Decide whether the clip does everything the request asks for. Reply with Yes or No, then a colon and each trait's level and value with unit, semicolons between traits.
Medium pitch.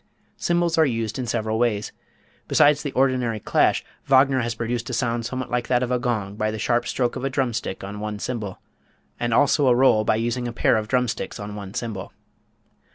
No: low, 120 Hz